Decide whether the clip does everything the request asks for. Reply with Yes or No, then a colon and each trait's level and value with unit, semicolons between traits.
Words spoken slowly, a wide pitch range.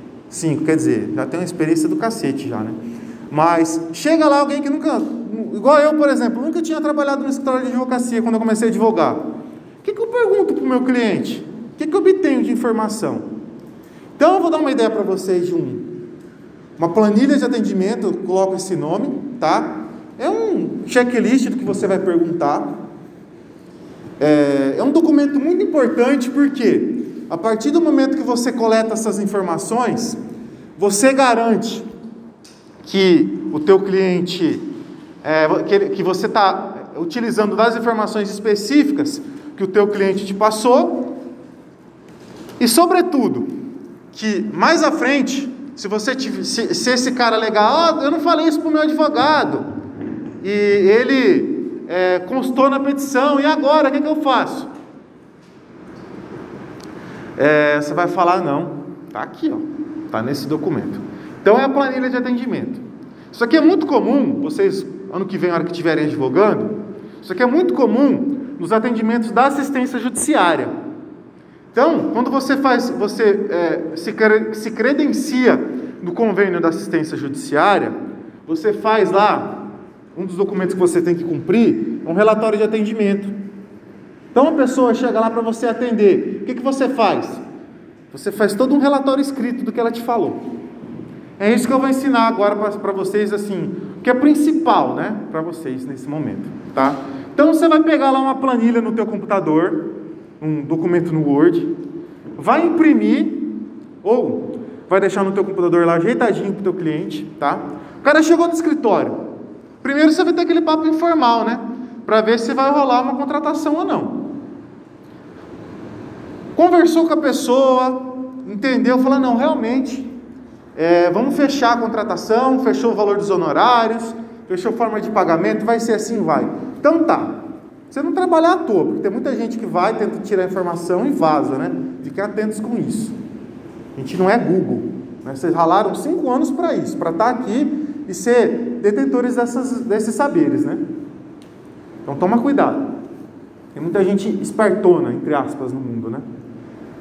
No: average, 165 wpm; wide, 6.1 semitones